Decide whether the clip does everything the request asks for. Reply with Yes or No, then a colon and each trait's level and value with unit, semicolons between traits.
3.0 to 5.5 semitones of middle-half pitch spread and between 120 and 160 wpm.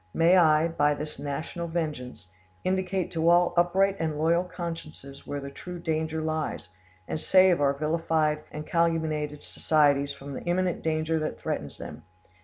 No: narrow, 2.5 semitones; average, 155 wpm